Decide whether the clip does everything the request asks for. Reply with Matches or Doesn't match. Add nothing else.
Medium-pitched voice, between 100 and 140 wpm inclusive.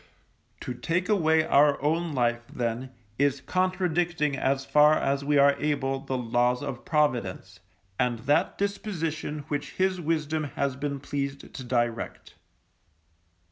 Matches